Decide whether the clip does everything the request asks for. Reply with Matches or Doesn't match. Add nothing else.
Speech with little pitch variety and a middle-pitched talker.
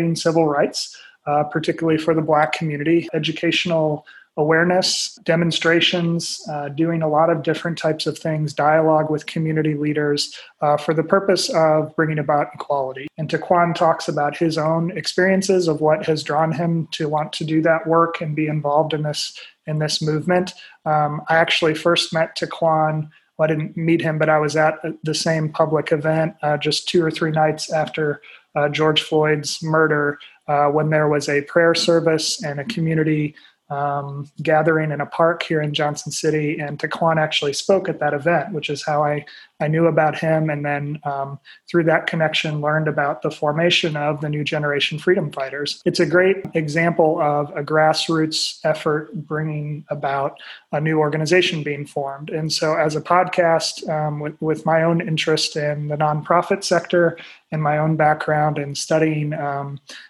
Matches